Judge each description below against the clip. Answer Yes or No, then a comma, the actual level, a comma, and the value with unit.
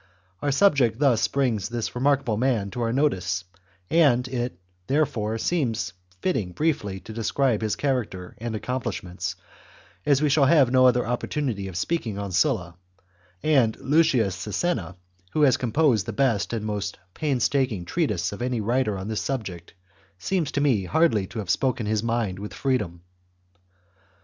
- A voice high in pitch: No, low, 120 Hz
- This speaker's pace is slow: No, average, 160 wpm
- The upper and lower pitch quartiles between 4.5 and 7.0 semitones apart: Yes, average, 5.1 semitones